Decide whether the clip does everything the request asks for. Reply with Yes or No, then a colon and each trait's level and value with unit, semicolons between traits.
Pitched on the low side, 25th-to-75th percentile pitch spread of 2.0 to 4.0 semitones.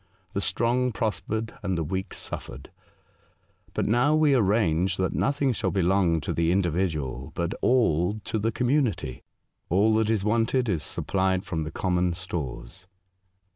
No: very low, 95 Hz; average, 4.9 semitones